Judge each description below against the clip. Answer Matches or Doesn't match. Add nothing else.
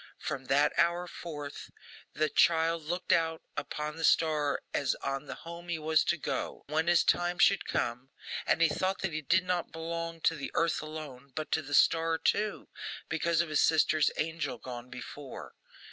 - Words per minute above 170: Matches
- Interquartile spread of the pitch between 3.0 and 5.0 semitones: Doesn't match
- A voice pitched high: Doesn't match